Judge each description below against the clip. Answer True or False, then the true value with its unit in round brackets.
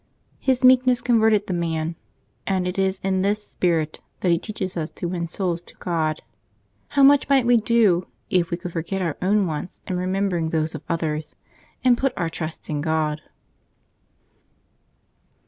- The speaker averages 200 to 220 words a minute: False (170 wpm)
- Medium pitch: True (180 Hz)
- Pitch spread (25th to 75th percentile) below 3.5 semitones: False (4.3 semitones)